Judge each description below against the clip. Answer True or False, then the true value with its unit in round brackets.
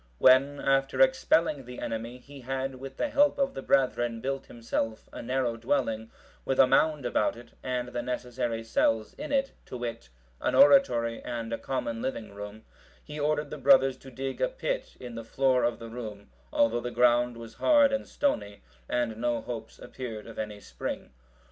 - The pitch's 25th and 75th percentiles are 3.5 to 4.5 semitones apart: False (2.9 semitones)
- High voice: False (125 Hz)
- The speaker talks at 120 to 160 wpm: False (185 wpm)